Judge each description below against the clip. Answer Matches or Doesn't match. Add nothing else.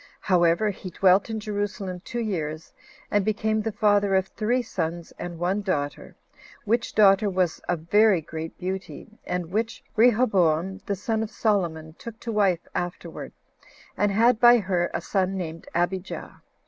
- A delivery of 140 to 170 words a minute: Matches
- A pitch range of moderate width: Matches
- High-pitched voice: Matches